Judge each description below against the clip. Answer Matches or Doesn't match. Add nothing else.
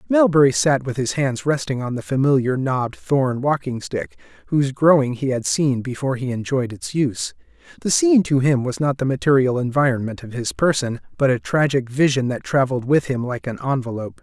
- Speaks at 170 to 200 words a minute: Matches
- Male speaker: Matches